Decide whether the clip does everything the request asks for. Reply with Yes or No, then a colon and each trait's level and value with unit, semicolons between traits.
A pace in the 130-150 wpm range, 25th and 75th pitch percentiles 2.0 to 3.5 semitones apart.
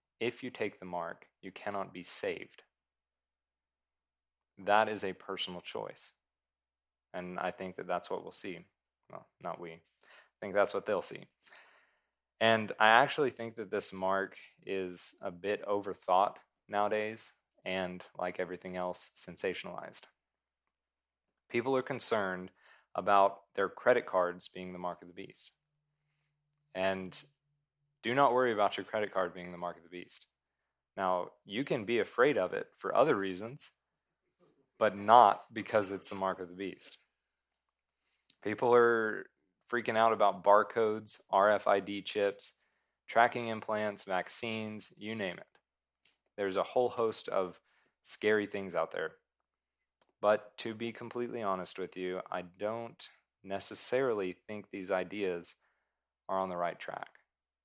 No: average, 140 wpm; average, 3.9 semitones